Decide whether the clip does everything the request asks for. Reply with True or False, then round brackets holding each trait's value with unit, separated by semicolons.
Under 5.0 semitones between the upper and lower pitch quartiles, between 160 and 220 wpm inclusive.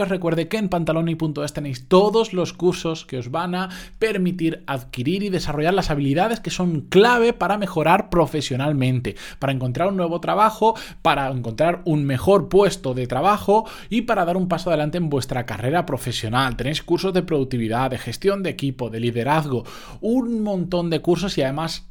False (5.4 semitones; 175 wpm)